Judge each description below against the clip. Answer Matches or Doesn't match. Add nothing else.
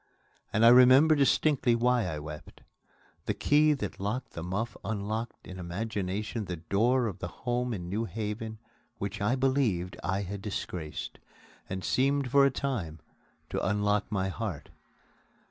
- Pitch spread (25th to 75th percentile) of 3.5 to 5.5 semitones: Matches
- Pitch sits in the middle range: Doesn't match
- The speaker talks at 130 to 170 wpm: Matches